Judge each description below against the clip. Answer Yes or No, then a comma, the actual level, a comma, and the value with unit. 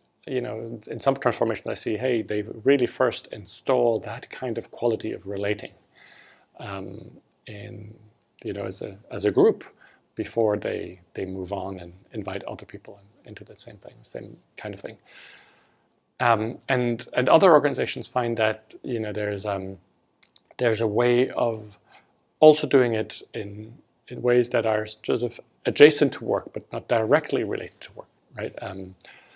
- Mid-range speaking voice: No, low, 110 Hz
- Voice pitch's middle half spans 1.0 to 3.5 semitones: Yes, average, 3.0 semitones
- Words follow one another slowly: No, average, 165 wpm